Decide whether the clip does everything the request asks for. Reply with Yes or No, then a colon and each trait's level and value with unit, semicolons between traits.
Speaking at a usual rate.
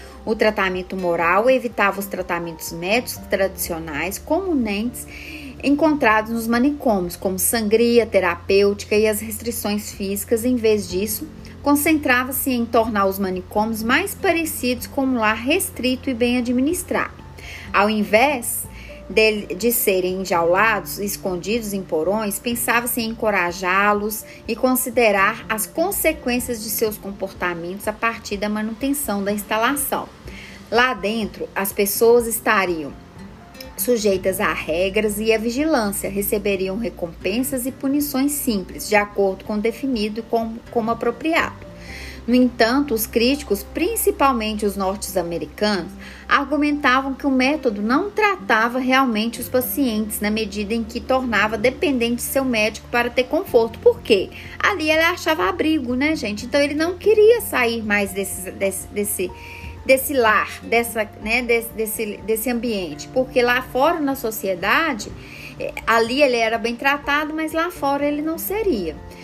Yes: average, 135 wpm